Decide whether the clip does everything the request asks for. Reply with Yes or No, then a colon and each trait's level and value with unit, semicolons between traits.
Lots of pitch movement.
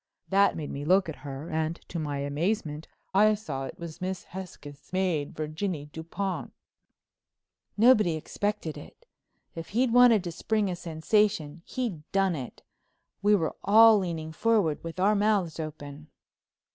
No: average, 4.7 semitones